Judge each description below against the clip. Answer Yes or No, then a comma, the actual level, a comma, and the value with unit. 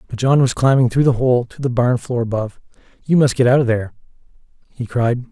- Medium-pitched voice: No, low, 125 Hz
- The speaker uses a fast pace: Yes, fast, 225 wpm